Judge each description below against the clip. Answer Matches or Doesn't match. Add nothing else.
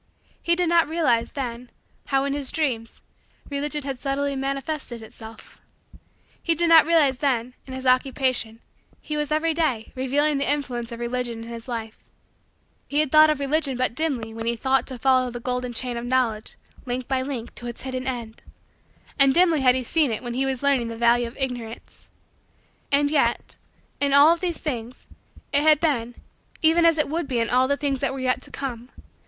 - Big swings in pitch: Doesn't match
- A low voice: Doesn't match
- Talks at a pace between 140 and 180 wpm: Doesn't match